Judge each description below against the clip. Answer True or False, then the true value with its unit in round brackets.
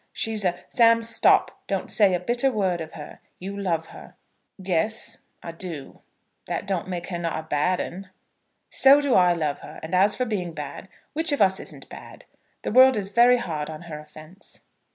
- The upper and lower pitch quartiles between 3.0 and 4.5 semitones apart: False (5.0 semitones)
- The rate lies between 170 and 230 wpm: True (195 wpm)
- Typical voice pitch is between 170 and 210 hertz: True (185 Hz)